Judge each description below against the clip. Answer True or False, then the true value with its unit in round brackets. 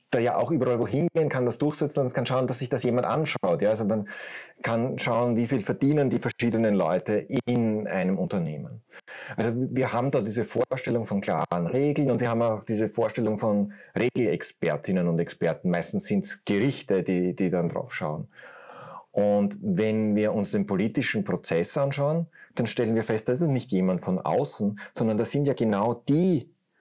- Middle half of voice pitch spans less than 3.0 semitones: False (4.4 semitones)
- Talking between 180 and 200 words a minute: True (185 wpm)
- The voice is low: True (120 Hz)